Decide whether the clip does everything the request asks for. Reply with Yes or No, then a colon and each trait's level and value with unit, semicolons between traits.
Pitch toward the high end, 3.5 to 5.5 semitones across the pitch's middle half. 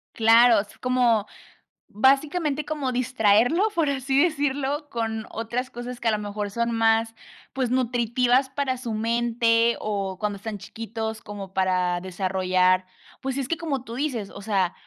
Yes: high, 230 Hz; average, 4.0 semitones